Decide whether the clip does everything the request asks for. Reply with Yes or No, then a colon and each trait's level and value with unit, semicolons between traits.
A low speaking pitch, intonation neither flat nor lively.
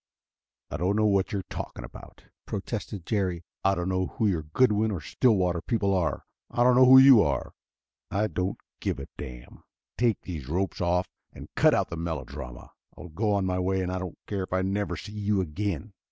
Yes: very low, 95 Hz; average, 3.1 semitones